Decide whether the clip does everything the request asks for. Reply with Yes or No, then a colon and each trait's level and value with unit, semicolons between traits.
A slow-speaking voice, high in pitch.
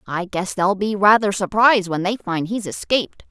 No: average, 200 wpm; high, 200 Hz